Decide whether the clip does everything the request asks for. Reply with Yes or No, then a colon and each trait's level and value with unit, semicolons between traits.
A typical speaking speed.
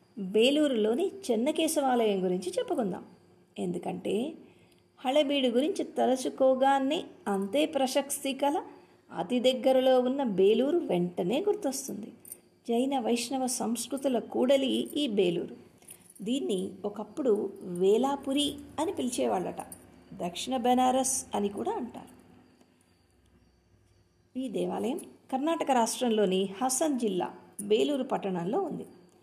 Yes: average, 85 wpm